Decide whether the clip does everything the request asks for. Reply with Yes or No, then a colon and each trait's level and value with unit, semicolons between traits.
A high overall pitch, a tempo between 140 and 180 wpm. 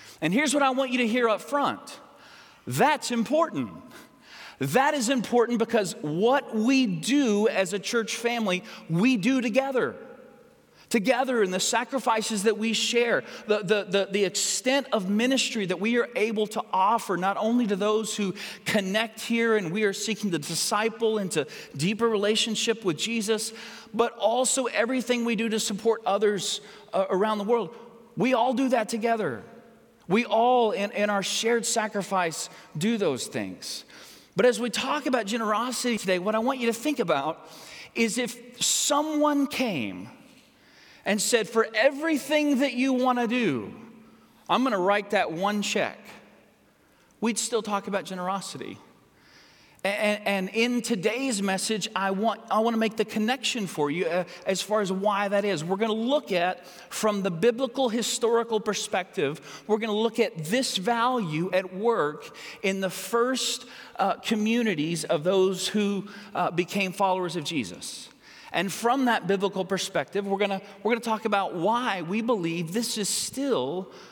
Yes: high, 220 Hz; average, 165 wpm